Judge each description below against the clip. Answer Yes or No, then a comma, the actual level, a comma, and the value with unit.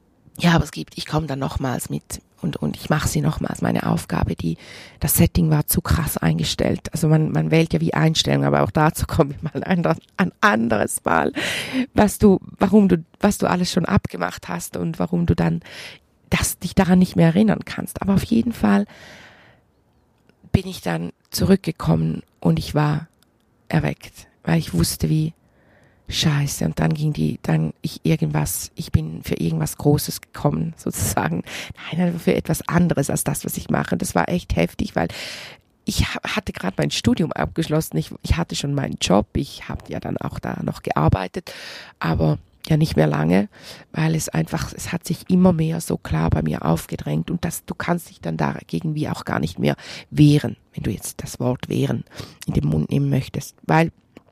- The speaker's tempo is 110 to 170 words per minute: No, fast, 190 wpm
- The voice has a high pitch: No, medium, 140 Hz